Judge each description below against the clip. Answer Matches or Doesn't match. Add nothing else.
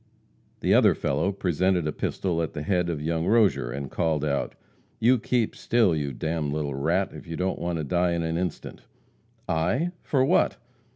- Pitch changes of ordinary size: Matches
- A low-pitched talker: Matches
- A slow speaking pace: Doesn't match